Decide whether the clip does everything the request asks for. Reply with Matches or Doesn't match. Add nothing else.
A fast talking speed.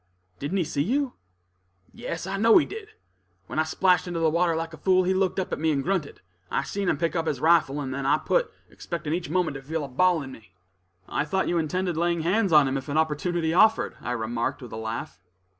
Matches